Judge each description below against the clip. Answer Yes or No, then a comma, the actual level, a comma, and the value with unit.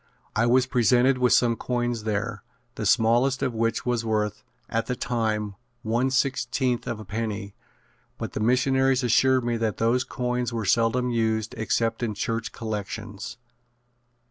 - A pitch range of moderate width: No, narrow, 2.2 semitones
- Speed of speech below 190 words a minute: Yes, average, 150 wpm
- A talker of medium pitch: No, low, 115 Hz